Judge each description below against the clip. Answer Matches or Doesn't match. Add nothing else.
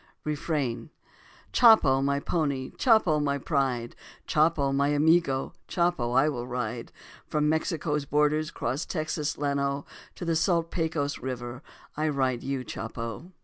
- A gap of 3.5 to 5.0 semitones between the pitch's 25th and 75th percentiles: Doesn't match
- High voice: Doesn't match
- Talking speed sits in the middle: Doesn't match